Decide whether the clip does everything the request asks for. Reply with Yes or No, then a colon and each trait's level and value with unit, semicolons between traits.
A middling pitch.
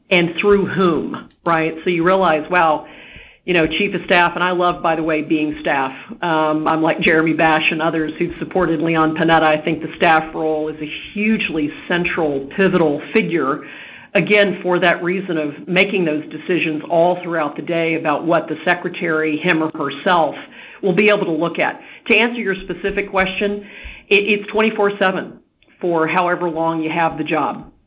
Yes: medium, 170 Hz